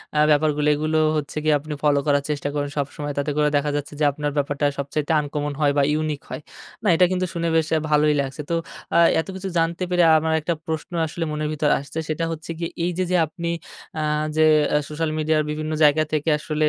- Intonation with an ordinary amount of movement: No, narrow, 1.6 semitones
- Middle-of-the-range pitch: Yes, medium, 150 Hz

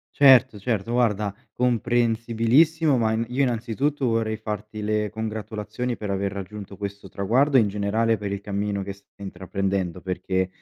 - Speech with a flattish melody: No, average, 3.0 semitones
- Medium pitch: No, low, 110 Hz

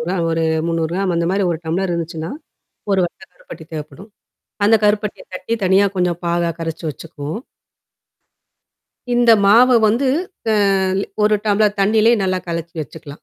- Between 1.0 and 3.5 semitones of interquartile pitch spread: No, average, 4.1 semitones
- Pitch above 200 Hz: No, medium, 185 Hz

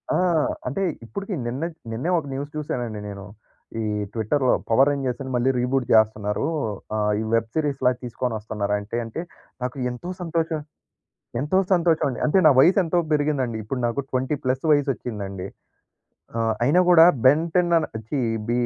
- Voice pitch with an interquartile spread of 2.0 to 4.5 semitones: No, average, 5.1 semitones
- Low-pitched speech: Yes, low, 130 Hz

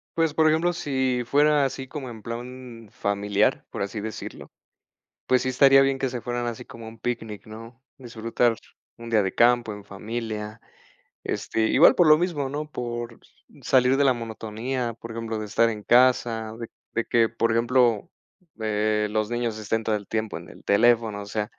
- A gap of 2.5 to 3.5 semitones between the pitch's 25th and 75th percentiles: Yes, average, 2.8 semitones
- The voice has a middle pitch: No, low, 115 Hz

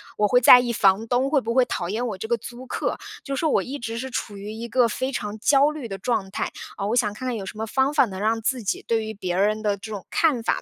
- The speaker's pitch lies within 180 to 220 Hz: No, high, 230 Hz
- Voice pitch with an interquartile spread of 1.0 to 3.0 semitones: No, average, 3.5 semitones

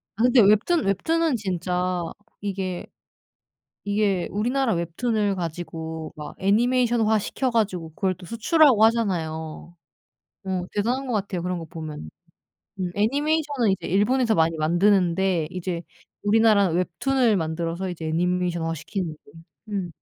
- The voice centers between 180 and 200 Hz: Yes, high, 190 Hz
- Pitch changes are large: No, average, 4.6 semitones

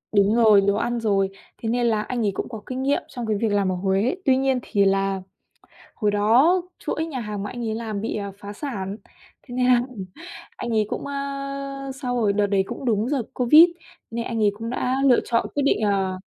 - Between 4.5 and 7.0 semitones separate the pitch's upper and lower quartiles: No, average, 3.9 semitones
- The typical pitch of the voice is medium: No, high, 230 Hz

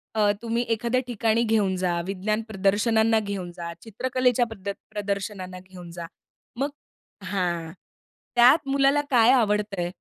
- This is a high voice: Yes, high, 210 Hz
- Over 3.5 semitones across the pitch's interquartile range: Yes, average, 3.9 semitones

